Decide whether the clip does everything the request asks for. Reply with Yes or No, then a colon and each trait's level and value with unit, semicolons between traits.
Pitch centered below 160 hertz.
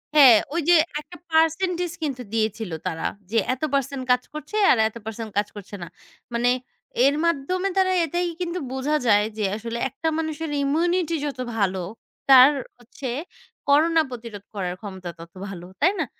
No: very high, 270 Hz